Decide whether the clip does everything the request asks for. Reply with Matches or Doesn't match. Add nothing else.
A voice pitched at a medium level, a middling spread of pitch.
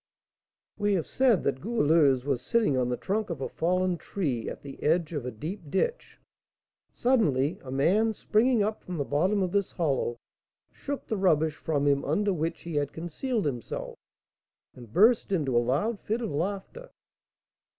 Doesn't match